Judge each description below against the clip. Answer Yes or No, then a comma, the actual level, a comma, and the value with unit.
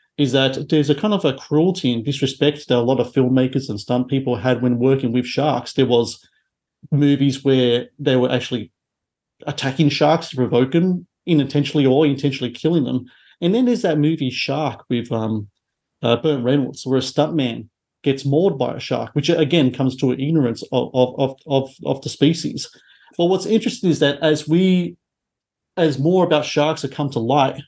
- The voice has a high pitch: No, medium, 140 Hz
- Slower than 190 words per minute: No, average, 195 wpm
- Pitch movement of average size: Yes, average, 3.4 semitones